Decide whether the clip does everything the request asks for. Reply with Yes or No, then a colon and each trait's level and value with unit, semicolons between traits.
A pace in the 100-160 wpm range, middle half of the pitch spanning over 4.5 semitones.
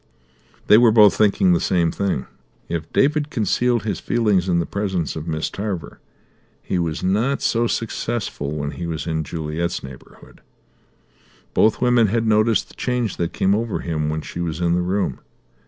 No: average, 170 wpm; average, 5.1 semitones